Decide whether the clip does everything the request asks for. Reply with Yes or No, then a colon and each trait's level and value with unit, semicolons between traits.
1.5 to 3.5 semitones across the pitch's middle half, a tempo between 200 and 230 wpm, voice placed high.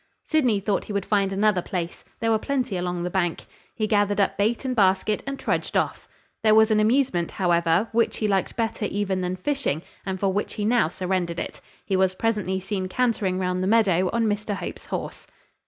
Yes: average, 3.0 semitones; fast, 205 wpm; high, 200 Hz